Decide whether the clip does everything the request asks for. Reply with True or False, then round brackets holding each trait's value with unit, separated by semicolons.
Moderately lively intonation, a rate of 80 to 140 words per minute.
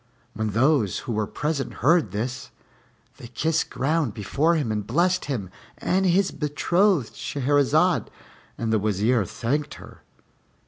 False (6.4 semitones; 135 wpm)